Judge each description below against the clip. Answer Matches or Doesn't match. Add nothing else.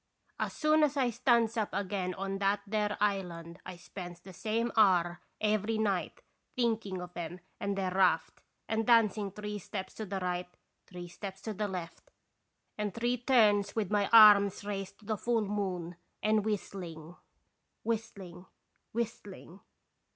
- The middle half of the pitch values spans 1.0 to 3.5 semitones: Matches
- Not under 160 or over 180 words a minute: Doesn't match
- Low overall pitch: Doesn't match